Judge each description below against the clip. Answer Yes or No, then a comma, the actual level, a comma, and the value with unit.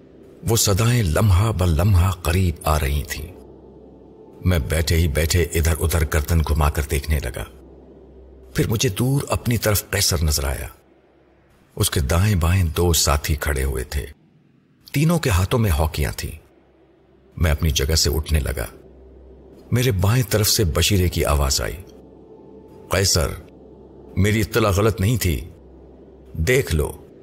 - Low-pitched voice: Yes, very low, 85 Hz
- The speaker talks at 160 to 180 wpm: No, average, 140 wpm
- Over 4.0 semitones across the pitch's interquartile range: Yes, average, 5.3 semitones